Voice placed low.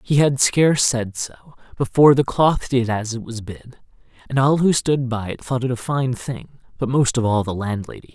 Yes: low, 125 Hz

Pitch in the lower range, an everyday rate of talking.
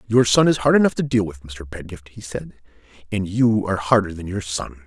No: low, 100 Hz; fast, 235 wpm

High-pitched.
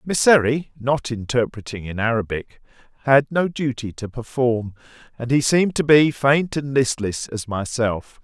No: low, 125 Hz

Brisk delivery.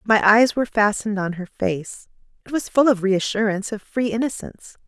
No: average, 185 wpm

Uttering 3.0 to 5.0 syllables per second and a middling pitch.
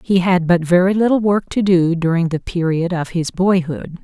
Yes: 4.9 syllables/s; medium, 175 Hz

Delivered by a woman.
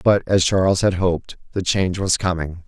No: male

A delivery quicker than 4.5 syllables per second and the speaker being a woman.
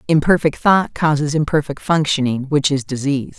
Yes: 5.3 syllables/s; female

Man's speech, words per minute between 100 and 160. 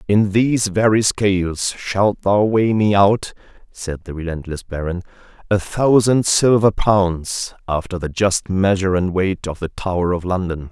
Yes: male; average, 155 wpm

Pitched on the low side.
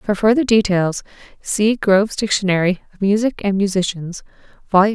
No: high, 200 Hz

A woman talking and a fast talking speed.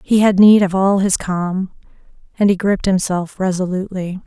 No: female; average, 170 wpm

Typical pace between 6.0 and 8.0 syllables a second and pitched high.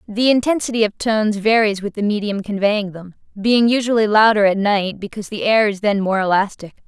No: 5.6 syllables/s; high, 210 Hz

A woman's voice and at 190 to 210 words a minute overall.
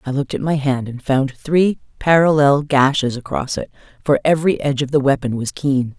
Yes: female; average, 200 wpm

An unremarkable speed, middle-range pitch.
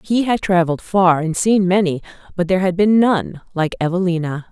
Yes: average, 185 wpm; medium, 180 Hz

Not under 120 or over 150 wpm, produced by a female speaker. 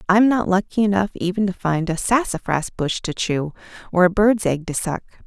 No: fast, 205 wpm; female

